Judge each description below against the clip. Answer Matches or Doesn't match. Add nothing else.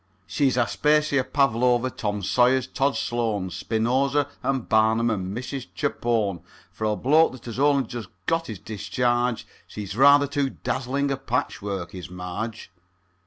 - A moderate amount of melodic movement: Matches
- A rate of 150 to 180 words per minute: Doesn't match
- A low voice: Matches